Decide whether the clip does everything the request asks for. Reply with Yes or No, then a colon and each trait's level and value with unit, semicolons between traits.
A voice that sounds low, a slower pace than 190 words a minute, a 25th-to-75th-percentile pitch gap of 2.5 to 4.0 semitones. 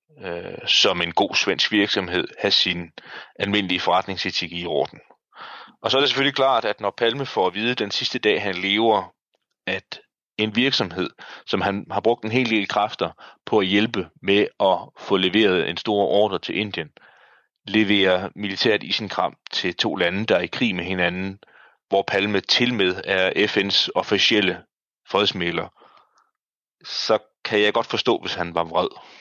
Yes: low, 105 Hz; average, 160 wpm; average, 3.2 semitones